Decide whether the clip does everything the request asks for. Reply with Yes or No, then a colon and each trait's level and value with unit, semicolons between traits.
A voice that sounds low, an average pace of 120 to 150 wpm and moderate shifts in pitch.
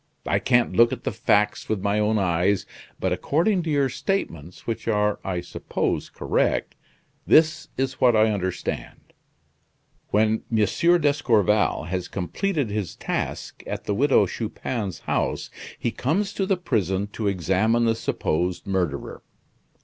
No: low, 110 Hz; average, 140 wpm; wide, 5.7 semitones